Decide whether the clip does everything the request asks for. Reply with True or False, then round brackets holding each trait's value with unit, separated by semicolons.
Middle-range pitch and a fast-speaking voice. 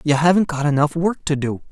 True (155 Hz; 245 wpm)